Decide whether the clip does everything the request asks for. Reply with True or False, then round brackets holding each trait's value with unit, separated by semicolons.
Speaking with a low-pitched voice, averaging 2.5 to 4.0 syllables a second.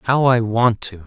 True (115 Hz; 3.9 syllables/s)